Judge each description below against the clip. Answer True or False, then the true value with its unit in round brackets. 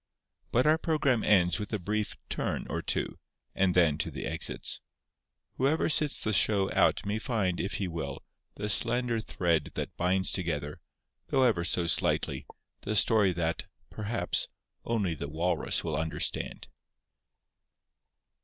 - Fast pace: False (145 wpm)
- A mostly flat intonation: False (4.8 semitones)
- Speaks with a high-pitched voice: False (95 Hz)